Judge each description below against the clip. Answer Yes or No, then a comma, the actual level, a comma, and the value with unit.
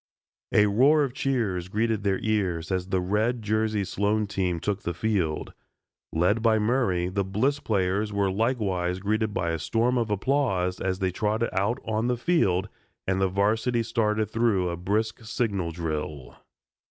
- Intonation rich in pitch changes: No, average, 3.4 semitones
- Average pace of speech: Yes, average, 165 wpm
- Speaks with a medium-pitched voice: No, low, 105 Hz